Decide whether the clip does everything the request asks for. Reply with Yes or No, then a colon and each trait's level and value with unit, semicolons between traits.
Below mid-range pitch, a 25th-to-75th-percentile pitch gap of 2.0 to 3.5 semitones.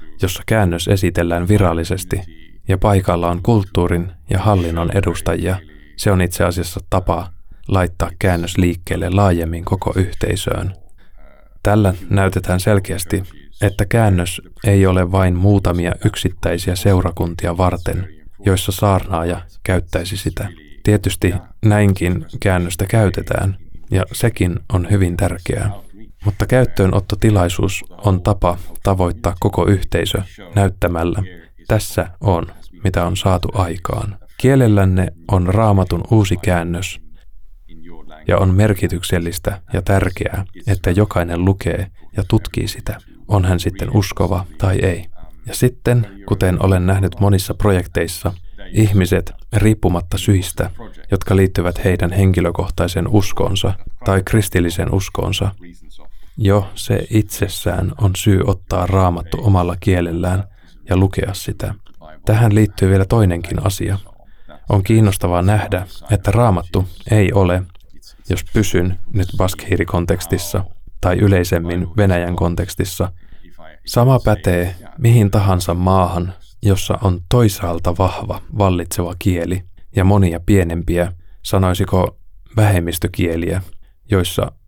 Yes: very low, 95 Hz; average, 2.7 semitones